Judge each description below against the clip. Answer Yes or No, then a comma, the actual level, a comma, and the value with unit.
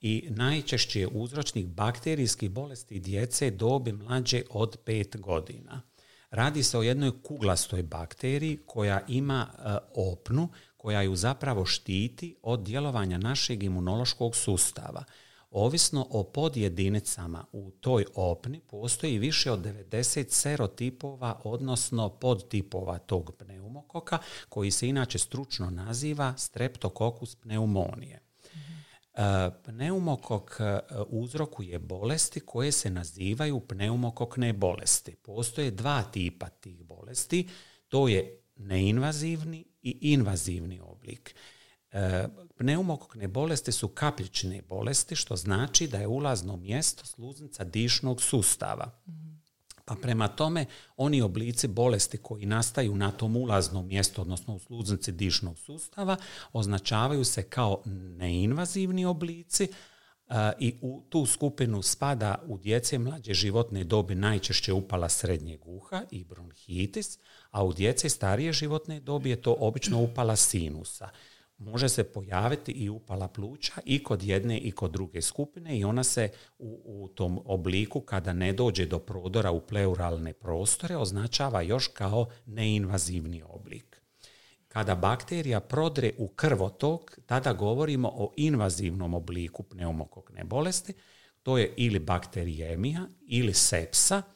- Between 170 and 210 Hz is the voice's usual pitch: No, low, 115 Hz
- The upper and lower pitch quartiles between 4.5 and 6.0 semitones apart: Yes, wide, 5.6 semitones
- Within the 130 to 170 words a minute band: No, average, 120 wpm